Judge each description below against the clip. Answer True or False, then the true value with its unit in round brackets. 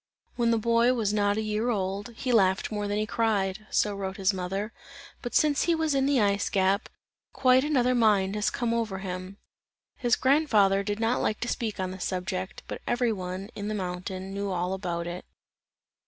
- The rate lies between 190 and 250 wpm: True (200 wpm)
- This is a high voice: True (205 Hz)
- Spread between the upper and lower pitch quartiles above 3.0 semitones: True (3.5 semitones)